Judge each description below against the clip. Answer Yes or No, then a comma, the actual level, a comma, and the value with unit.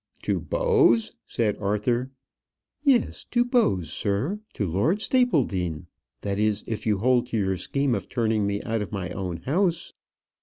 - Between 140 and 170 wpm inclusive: Yes, average, 155 wpm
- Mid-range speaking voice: No, low, 110 Hz